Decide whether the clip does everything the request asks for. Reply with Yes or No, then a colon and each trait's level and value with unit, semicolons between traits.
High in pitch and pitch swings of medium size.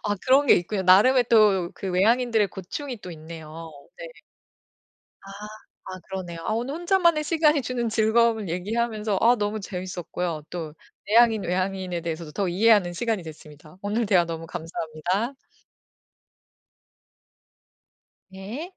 Yes: high, 200 Hz; average, 5.0 semitones